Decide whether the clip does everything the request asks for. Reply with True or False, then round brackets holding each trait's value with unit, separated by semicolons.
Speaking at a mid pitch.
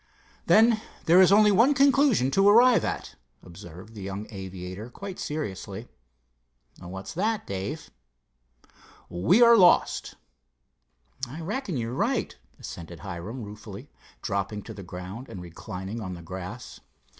False (110 Hz)